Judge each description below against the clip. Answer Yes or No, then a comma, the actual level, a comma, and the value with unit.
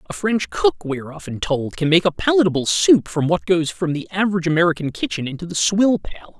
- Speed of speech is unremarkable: No, fast, 225 wpm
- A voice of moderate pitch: Yes, medium, 170 Hz